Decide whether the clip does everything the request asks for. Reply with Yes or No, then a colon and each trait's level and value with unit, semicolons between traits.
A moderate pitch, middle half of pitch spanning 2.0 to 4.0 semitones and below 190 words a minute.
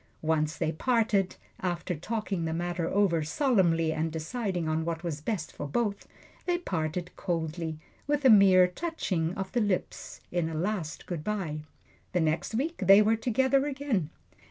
No: medium, 180 Hz; average, 5.1 semitones; average, 160 wpm